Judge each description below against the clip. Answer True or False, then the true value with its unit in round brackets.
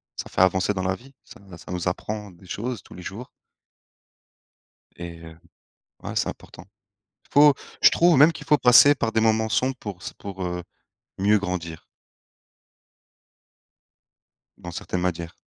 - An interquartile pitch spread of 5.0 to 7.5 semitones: True (5.6 semitones)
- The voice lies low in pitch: True (100 Hz)